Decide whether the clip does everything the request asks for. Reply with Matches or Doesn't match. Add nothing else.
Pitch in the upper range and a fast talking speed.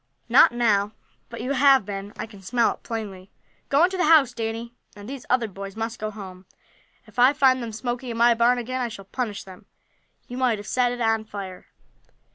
Matches